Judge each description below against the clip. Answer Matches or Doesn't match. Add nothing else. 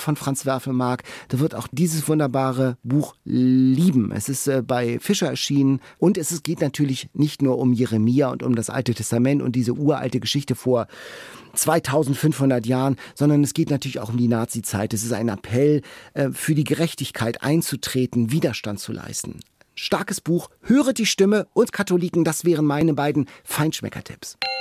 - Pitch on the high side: Doesn't match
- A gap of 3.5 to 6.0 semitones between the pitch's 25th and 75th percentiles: Matches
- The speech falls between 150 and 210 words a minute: Matches